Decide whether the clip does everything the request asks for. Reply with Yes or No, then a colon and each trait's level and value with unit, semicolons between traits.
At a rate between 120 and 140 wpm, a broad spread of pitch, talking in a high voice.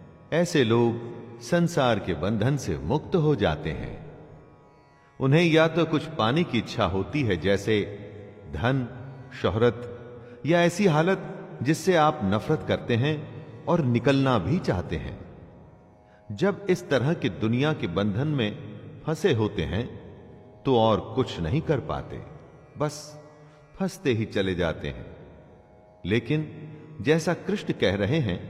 No: average, 135 wpm; wide, 6.4 semitones; low, 130 Hz